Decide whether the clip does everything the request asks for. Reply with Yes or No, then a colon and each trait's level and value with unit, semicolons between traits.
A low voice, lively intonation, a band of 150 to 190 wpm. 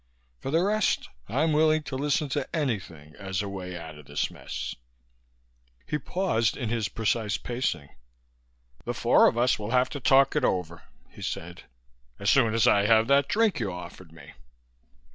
Yes: low, 115 Hz; wide, 7.4 semitones; average, 175 wpm